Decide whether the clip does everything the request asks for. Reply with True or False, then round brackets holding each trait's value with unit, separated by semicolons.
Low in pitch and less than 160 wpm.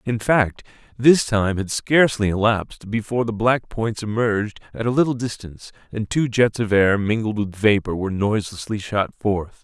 False (110 Hz; 175 wpm)